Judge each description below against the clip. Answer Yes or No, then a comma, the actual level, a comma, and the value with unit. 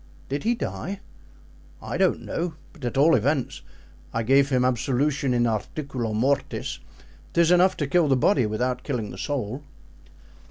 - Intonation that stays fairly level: No, average, 3.8 semitones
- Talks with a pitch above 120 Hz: Yes, low, 135 Hz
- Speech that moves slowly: No, average, 155 wpm